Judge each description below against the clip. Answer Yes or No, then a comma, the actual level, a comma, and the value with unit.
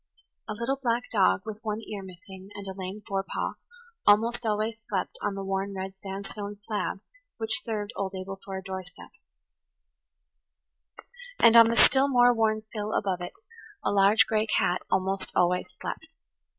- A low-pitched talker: No, high, 205 Hz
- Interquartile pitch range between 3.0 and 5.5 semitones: No, narrow, 2.6 semitones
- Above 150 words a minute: Yes, average, 160 wpm